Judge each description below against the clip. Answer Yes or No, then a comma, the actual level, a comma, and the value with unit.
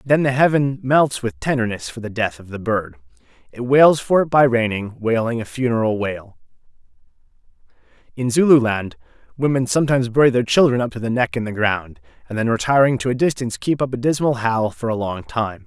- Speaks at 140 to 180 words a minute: No, average, 195 wpm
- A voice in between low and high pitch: No, low, 120 Hz